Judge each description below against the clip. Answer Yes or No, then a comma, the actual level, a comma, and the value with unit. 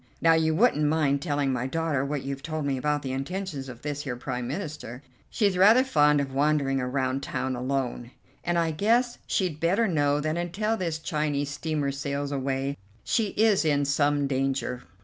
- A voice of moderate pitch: Yes, medium, 145 Hz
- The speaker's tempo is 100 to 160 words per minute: No, average, 180 wpm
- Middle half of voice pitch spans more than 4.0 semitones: No, average, 3.2 semitones